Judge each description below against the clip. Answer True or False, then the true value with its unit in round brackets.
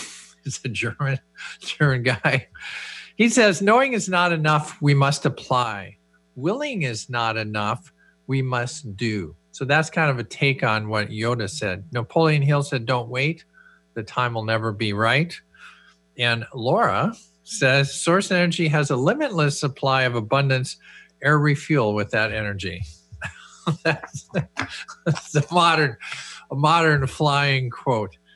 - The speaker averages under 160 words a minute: True (140 wpm)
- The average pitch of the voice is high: False (135 Hz)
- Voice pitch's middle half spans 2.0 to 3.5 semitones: False (5.3 semitones)